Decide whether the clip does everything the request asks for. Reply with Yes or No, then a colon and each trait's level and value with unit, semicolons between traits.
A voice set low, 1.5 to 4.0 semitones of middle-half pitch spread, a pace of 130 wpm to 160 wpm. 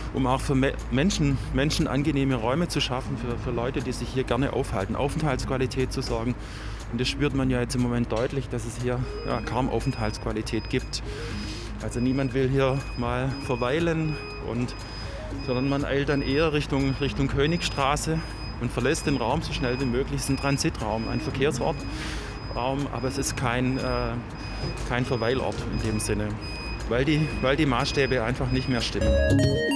No: low, 125 Hz; average, 3.1 semitones; average, 170 wpm